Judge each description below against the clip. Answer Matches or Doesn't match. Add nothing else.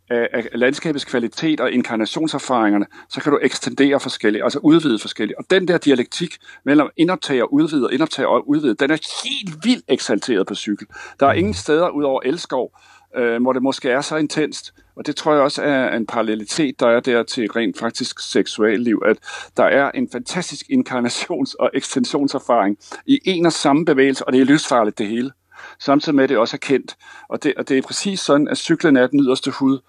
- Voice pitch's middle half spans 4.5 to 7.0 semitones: Matches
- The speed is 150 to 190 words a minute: Doesn't match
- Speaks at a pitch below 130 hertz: Doesn't match